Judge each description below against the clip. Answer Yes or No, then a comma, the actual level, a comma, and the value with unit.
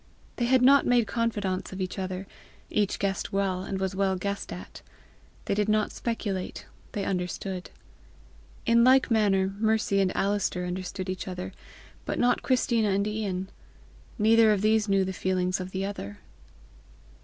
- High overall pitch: Yes, high, 195 Hz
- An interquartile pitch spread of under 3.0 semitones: Yes, narrow, 2.6 semitones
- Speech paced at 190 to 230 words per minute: No, average, 155 wpm